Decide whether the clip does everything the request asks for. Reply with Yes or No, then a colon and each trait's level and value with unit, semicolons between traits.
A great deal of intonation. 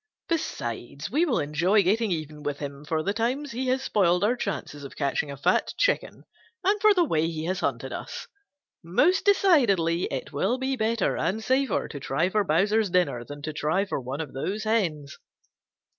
Yes: wide, 7.9 semitones